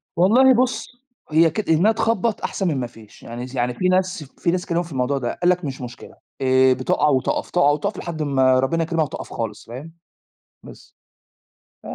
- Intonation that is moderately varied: No, wide, 5.7 semitones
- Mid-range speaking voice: Yes, medium, 155 Hz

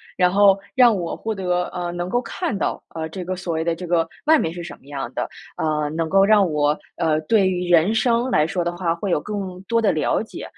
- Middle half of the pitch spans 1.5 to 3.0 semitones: No, average, 3.7 semitones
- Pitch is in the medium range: Yes, medium, 180 Hz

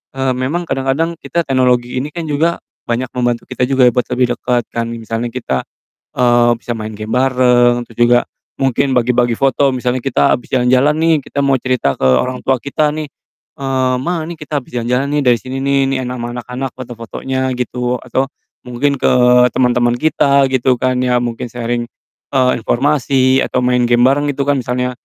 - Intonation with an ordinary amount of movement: No, narrow, 1.8 semitones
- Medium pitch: No, low, 125 Hz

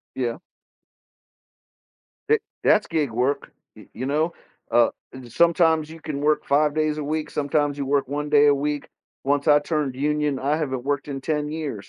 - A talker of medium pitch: Yes, medium, 145 Hz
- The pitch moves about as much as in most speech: No, narrow, 1.7 semitones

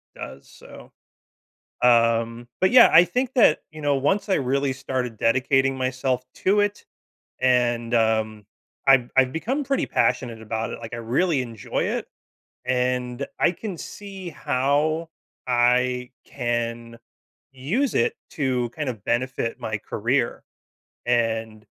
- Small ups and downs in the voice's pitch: No, average, 4.1 semitones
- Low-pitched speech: Yes, low, 125 Hz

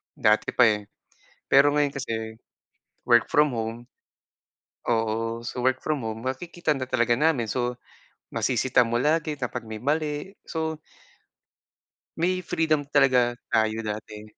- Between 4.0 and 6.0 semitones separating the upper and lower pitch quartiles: Yes, average, 4.7 semitones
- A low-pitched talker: Yes, low, 125 Hz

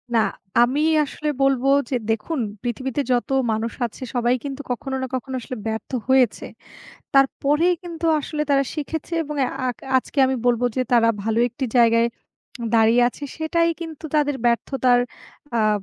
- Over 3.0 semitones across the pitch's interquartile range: Yes, average, 3.5 semitones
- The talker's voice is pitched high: Yes, very high, 260 Hz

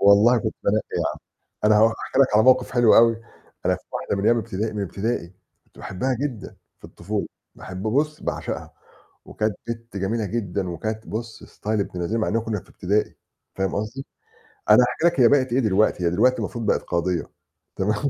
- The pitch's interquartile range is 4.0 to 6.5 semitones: No, average, 3.0 semitones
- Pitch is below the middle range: Yes, low, 110 Hz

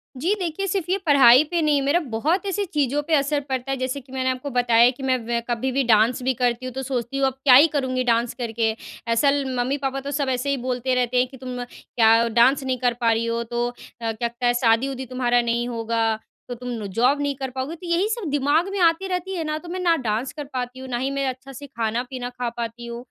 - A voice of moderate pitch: No, very high, 260 Hz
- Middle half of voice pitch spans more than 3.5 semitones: No, average, 3.0 semitones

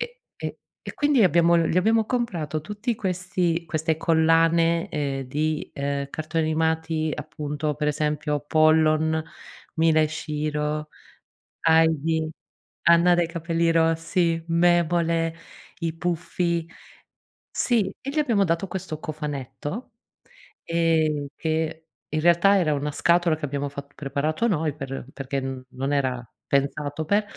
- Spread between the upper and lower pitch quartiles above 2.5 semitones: No, narrow, 2.2 semitones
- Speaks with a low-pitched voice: No, medium, 160 Hz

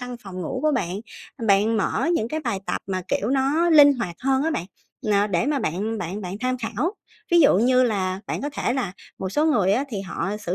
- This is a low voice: No, high, 225 Hz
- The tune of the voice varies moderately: No, wide, 5.8 semitones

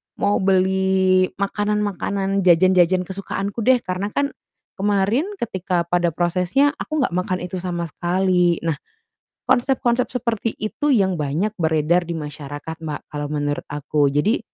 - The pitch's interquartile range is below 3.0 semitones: No, average, 3.3 semitones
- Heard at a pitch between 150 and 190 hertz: Yes, medium, 185 Hz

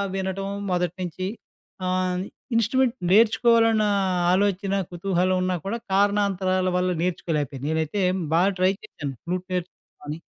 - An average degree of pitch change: No, narrow, 2.1 semitones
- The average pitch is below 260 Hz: Yes, medium, 185 Hz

